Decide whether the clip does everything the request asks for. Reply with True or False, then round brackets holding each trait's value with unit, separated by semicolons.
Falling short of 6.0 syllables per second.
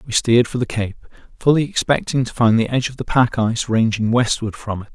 False (6.1 syllables/s)